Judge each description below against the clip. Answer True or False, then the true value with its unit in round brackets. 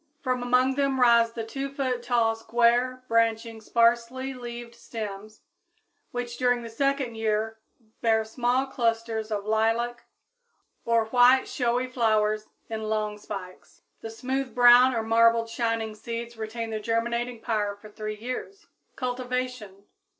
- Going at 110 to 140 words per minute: True (135 wpm)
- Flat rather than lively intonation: True (2.0 semitones)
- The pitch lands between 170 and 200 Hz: False (235 Hz)